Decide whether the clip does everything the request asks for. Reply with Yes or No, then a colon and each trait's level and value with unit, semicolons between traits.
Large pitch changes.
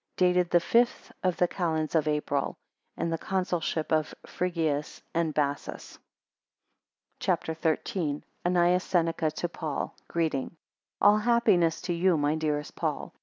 No: narrow, 2.5 semitones